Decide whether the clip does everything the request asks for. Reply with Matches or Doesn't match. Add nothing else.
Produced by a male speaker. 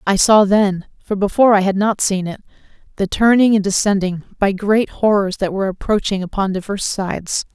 Doesn't match